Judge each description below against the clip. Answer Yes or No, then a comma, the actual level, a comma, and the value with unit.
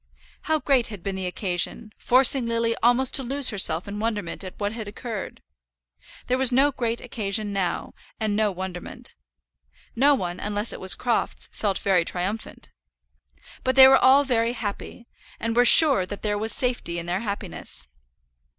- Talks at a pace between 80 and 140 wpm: No, average, 170 wpm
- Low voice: No, high, 220 Hz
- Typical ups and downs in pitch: Yes, average, 4.1 semitones